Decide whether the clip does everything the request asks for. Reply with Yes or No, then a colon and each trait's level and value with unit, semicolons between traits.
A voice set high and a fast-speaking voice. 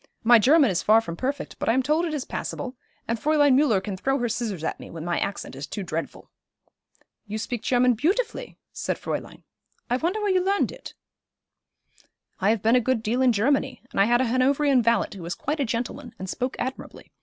Yes: high, 245 Hz; fast, 215 wpm